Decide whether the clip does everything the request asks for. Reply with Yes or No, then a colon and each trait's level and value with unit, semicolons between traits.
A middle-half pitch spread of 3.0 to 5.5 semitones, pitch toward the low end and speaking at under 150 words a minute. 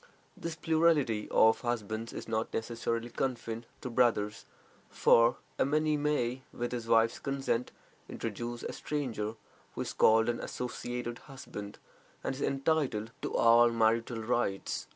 No: narrow, 2.6 semitones; low, 120 Hz; slow, 135 wpm